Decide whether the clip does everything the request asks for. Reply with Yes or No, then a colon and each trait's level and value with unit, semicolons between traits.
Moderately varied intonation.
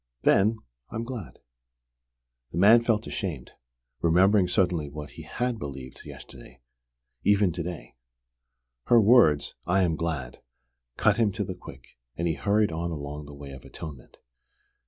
No: wide, 5.8 semitones